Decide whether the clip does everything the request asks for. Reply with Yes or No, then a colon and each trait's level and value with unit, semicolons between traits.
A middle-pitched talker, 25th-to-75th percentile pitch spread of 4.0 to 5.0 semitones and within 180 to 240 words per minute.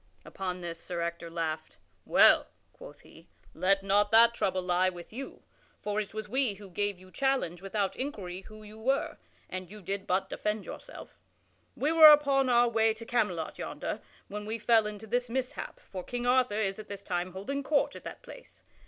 No: high, 210 Hz; average, 4.4 semitones; average, 190 wpm